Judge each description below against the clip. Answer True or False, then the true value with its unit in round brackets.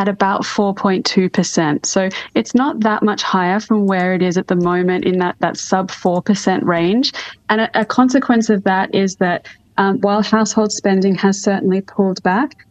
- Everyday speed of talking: True (180 wpm)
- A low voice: False (195 Hz)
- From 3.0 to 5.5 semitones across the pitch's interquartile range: False (2.5 semitones)